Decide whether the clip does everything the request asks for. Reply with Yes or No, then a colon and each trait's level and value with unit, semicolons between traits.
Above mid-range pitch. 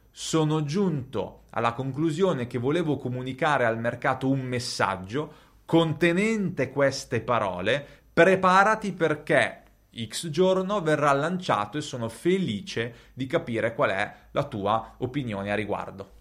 No: low, 135 Hz